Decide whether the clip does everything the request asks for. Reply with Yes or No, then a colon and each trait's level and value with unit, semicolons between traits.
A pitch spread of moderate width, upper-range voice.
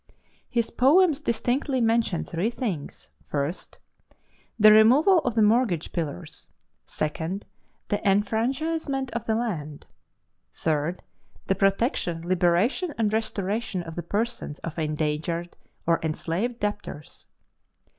No: wide, 6.2 semitones; high, 205 Hz